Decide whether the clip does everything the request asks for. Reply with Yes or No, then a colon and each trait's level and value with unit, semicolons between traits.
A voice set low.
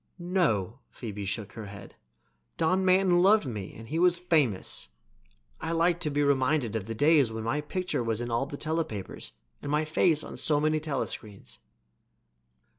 No: medium, 145 Hz